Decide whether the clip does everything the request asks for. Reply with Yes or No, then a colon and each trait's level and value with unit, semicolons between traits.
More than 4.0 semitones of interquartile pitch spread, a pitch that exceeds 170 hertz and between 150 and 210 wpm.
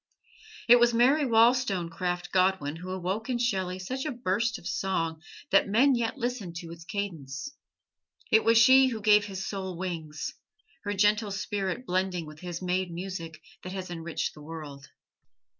Yes: average, 4.8 semitones; high, 190 Hz; average, 160 wpm